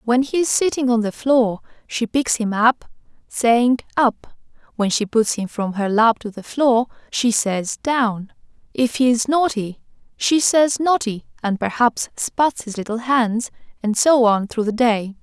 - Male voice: No, female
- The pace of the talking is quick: No, average, 175 wpm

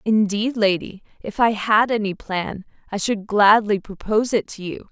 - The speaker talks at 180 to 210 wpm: No, average, 170 wpm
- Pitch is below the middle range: No, high, 210 Hz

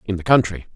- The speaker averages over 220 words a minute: Yes, fast, 240 wpm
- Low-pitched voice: Yes, low, 100 Hz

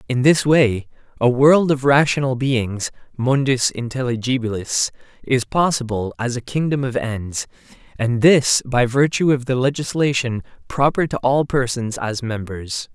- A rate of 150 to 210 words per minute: No, average, 140 wpm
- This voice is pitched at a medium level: No, low, 125 Hz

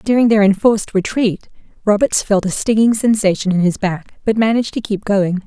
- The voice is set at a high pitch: Yes, high, 210 Hz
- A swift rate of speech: No, average, 185 wpm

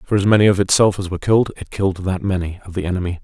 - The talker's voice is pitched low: Yes, very low, 95 Hz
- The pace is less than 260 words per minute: No, fast, 280 wpm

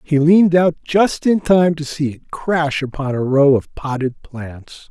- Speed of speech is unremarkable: Yes, average, 195 wpm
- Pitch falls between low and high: Yes, medium, 150 Hz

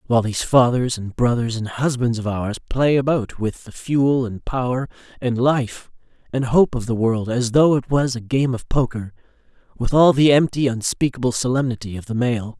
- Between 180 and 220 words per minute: Yes, average, 190 wpm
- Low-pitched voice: Yes, low, 125 Hz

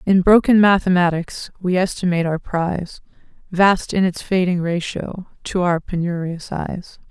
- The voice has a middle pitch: Yes, medium, 180 Hz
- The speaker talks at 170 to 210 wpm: No, slow, 135 wpm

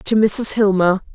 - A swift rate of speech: No, average, 155 wpm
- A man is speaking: No, female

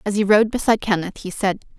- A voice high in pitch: Yes, high, 205 Hz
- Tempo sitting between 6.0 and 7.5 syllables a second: Yes, 6.4 syllables/s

